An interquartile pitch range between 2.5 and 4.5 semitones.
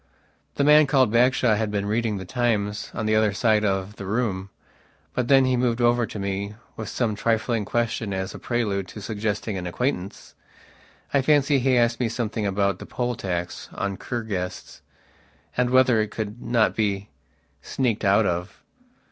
Yes: average, 3.3 semitones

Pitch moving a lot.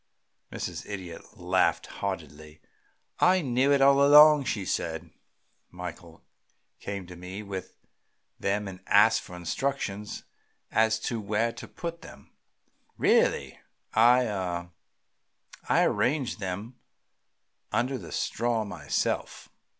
Yes: wide, 5.7 semitones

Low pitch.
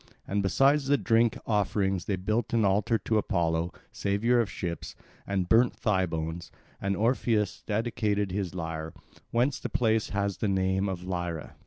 Yes: low, 100 Hz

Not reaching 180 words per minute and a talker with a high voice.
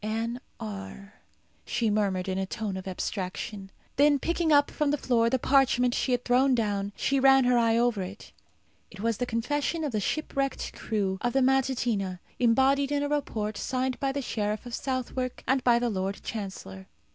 No: average, 185 wpm; high, 240 Hz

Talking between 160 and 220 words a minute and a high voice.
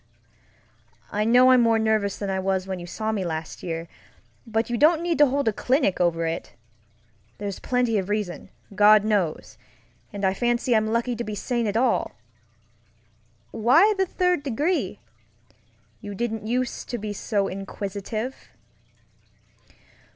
No: average, 150 wpm; high, 220 Hz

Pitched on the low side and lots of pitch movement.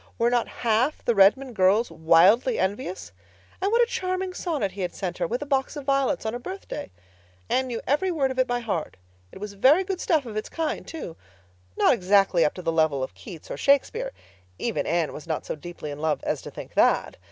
No: high, 230 Hz; wide, 7.9 semitones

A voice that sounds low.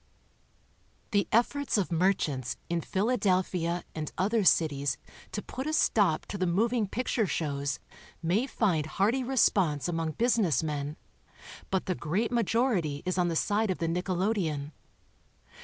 No: medium, 185 Hz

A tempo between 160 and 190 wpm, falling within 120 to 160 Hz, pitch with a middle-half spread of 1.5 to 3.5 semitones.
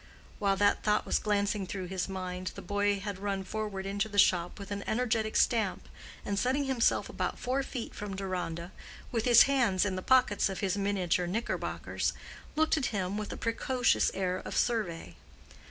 No: average, 180 wpm; high, 205 Hz; average, 3.1 semitones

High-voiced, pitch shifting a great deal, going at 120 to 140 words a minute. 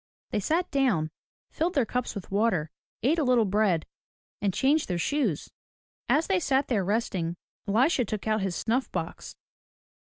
No: high, 225 Hz; wide, 6.0 semitones; average, 160 wpm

